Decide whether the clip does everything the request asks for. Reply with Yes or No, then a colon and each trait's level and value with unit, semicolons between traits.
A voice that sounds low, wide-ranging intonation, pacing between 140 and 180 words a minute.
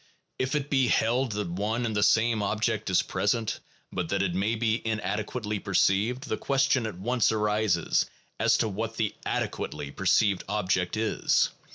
No: low, 110 Hz; average, 2.7 semitones; average, 165 wpm